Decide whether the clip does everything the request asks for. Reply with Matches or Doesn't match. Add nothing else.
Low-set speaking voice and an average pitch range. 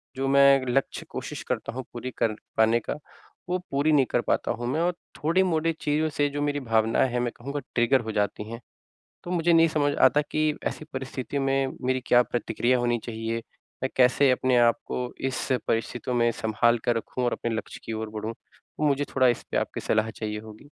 Matches